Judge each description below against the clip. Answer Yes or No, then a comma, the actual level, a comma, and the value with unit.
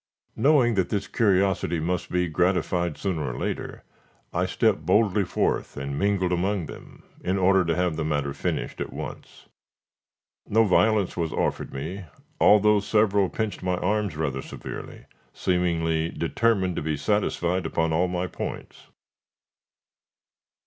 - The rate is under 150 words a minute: Yes, average, 140 wpm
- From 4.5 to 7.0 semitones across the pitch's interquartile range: No, average, 3.6 semitones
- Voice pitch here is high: No, very low, 90 Hz